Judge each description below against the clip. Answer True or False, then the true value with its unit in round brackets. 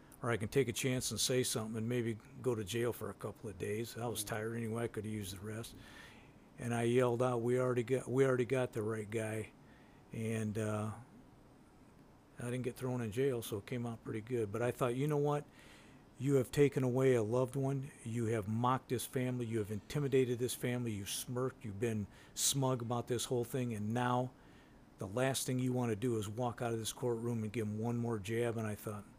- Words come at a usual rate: False (230 wpm)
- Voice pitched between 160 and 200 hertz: False (120 Hz)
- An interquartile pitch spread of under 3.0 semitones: True (2.5 semitones)